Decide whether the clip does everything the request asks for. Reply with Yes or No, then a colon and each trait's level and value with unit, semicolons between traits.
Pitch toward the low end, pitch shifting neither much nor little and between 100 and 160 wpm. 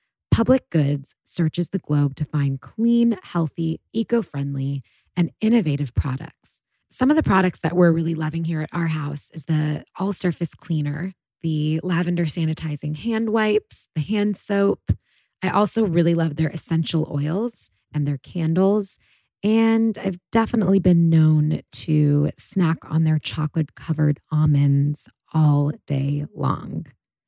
No: medium, 160 Hz; average, 4.2 semitones; slow, 135 wpm